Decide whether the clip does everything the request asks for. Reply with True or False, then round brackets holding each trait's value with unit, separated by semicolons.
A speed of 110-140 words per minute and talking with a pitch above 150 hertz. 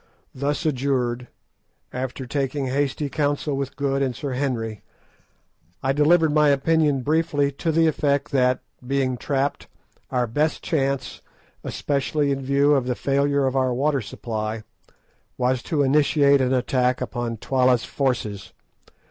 False (135 wpm; 135 Hz)